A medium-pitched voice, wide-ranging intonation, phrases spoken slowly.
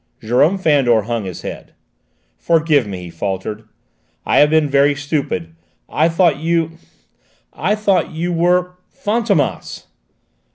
Yes: medium, 150 Hz; wide, 6.6 semitones; slow, 125 wpm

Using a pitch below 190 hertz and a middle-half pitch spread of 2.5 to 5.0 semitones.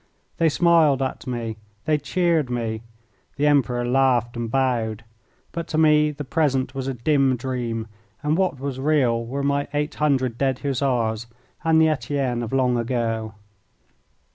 Yes: low, 135 Hz; average, 3.7 semitones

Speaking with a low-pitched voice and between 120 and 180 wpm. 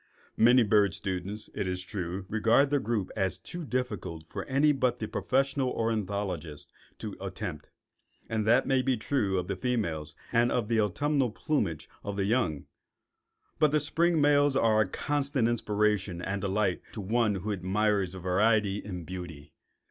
Yes: low, 105 Hz; average, 160 wpm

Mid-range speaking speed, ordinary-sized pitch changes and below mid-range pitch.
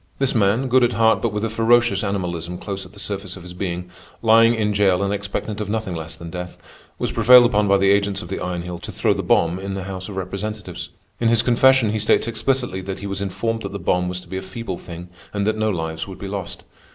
No: fast, 255 wpm; average, 3.3 semitones; low, 100 Hz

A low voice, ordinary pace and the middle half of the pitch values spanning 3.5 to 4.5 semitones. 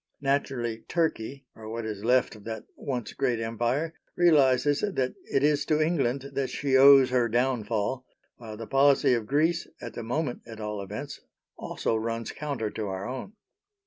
Yes: low, 125 Hz; average, 170 wpm; average, 3.9 semitones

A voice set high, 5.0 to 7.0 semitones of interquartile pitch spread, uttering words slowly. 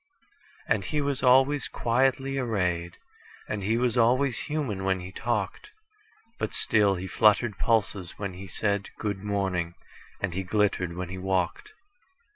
No: low, 105 Hz; wide, 5.4 semitones; slow, 130 wpm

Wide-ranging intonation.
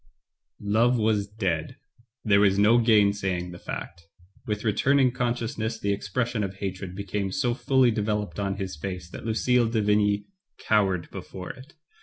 No: average, 2.9 semitones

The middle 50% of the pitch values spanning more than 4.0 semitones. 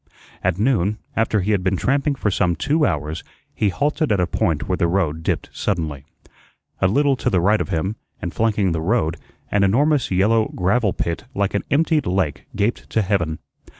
Yes: average, 4.6 semitones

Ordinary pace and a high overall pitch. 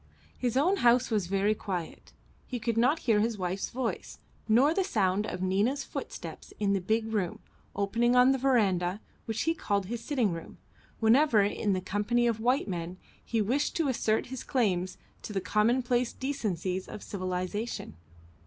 Yes: average, 170 wpm; high, 220 Hz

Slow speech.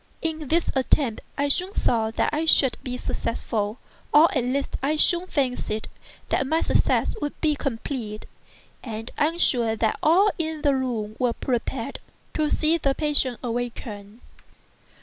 No: average, 150 wpm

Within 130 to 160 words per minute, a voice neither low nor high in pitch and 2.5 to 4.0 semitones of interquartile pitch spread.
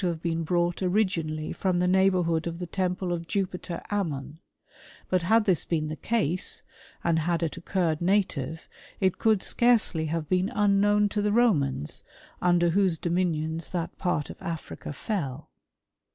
Yes: average, 155 wpm; medium, 175 Hz; average, 3.0 semitones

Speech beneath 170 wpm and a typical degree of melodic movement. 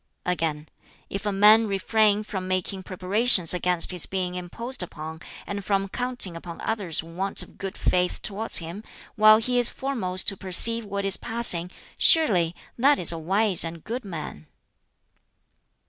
Yes: average, 155 wpm; average, 3.4 semitones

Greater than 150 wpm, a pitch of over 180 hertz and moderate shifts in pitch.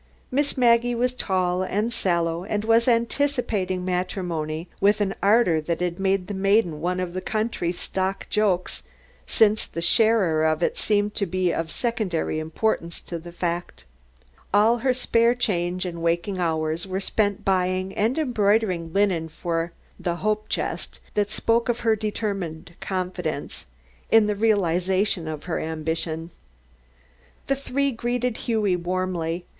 No: average, 145 wpm; high, 190 Hz; average, 4.2 semitones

